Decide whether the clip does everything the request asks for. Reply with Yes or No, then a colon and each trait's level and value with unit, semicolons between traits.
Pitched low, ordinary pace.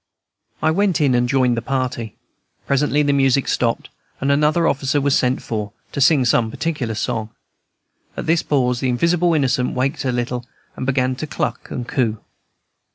Yes: low, 130 Hz; average, 170 wpm